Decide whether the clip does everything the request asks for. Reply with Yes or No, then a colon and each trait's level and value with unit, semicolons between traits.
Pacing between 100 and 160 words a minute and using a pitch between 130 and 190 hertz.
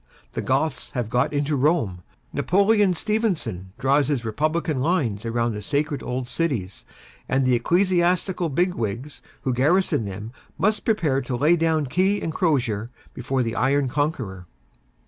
Yes: average, 145 wpm; medium, 140 Hz